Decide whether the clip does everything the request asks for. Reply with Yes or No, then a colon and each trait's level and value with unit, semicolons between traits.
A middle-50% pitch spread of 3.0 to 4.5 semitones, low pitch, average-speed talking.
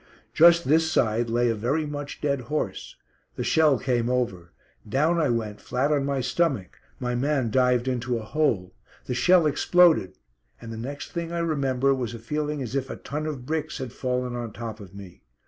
Yes: average, 4.2 semitones; low, 130 Hz; average, 195 wpm